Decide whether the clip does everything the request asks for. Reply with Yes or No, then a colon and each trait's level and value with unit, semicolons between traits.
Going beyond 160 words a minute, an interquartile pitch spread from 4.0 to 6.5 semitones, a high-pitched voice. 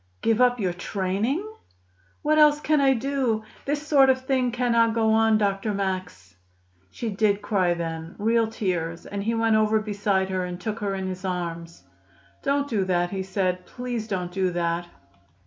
Yes: average, 175 wpm; average, 4.3 semitones; high, 210 Hz